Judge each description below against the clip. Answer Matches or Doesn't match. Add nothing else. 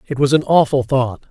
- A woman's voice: Doesn't match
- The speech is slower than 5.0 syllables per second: Doesn't match